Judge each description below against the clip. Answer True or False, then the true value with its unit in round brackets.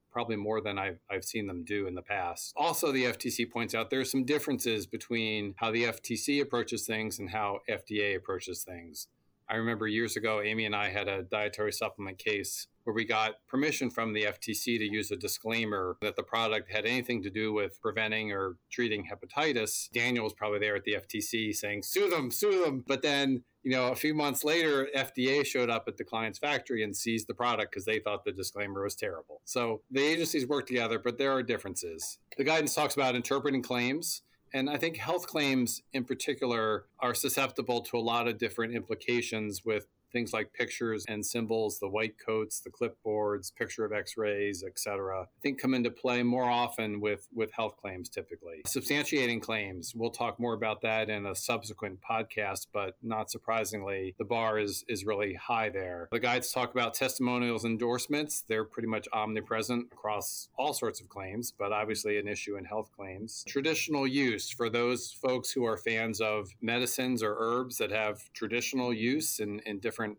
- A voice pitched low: True (115 Hz)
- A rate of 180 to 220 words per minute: True (190 wpm)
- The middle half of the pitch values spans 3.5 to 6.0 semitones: False (2.8 semitones)